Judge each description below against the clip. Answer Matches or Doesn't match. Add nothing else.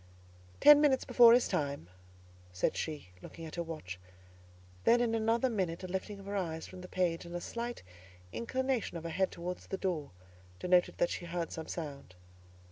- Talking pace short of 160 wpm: Doesn't match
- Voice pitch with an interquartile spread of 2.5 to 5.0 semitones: Doesn't match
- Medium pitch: Matches